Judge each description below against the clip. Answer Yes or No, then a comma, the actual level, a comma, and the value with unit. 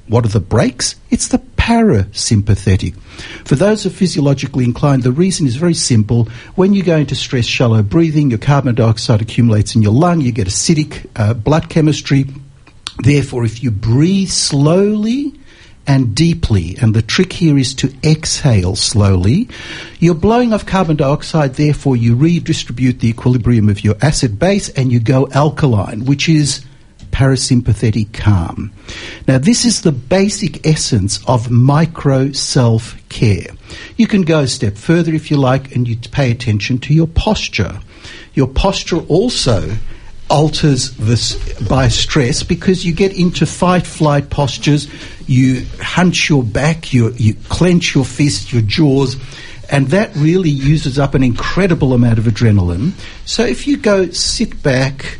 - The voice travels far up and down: Yes, wide, 5.7 semitones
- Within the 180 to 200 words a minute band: No, average, 155 wpm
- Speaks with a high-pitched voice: No, low, 135 Hz